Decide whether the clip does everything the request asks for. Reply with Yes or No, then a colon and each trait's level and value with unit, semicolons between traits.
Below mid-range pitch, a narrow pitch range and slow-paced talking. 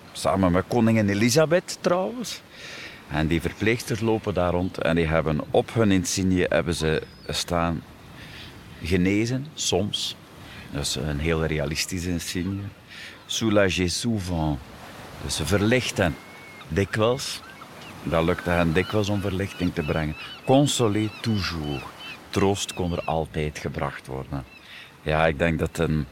No: very low, 90 Hz; average, 4.6 semitones; slow, 125 wpm